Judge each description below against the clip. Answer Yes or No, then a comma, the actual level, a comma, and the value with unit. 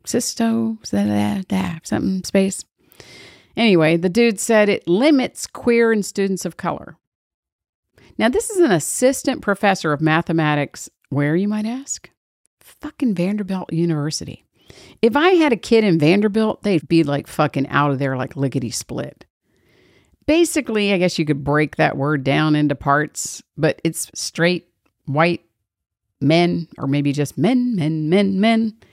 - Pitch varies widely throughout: Yes, wide, 6.9 semitones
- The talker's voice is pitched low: No, medium, 175 Hz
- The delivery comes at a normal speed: Yes, average, 150 wpm